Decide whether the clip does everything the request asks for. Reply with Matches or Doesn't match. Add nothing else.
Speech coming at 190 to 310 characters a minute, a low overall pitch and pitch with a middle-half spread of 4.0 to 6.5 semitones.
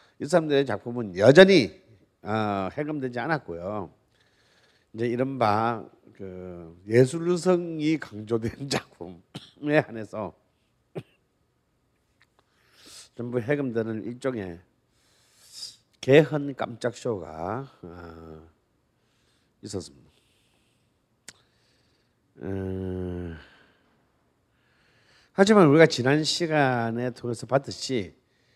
Doesn't match